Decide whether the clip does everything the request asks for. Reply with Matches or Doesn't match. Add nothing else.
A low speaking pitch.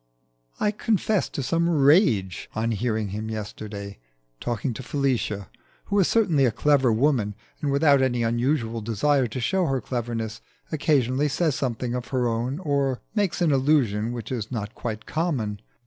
Matches